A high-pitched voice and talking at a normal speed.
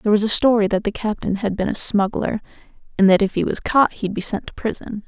No: high, 205 Hz; fast, 260 wpm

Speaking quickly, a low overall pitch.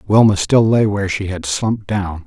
Yes: fast, 210 wpm; low, 100 Hz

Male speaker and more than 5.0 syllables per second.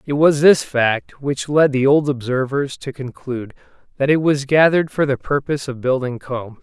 No: male; 4.9 syllables/s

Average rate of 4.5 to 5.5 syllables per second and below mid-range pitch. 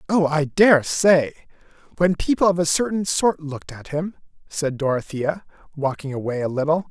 No: 5.0 syllables/s; medium, 160 Hz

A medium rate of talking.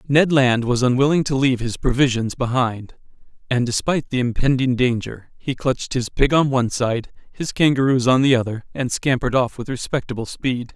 Yes: average, 180 wpm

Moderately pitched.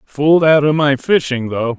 Yes: medium, 145 Hz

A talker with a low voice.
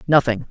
Yes: low, 130 Hz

